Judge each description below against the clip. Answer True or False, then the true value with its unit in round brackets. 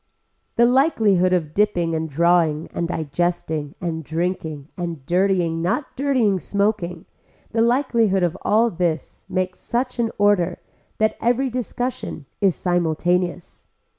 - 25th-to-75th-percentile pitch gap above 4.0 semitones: True (4.7 semitones)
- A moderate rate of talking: False (125 wpm)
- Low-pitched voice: False (180 Hz)